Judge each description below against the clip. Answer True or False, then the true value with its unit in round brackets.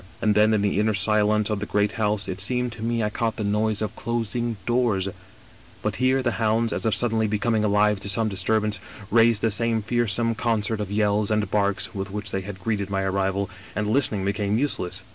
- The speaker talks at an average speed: False (210 wpm)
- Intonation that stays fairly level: True (2.0 semitones)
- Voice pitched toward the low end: True (105 Hz)